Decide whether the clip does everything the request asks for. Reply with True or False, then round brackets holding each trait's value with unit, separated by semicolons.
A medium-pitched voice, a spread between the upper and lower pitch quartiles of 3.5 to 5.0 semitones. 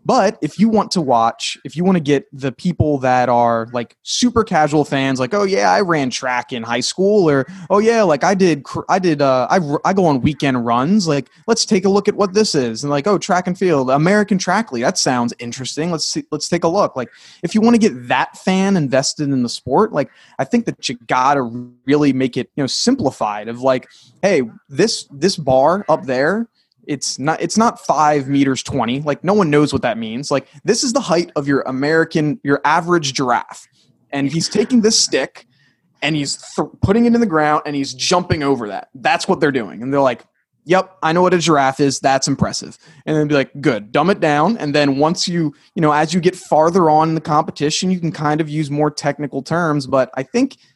False (150 Hz; 5.4 semitones)